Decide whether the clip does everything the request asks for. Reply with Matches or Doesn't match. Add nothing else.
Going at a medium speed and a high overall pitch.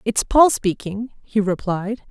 Matches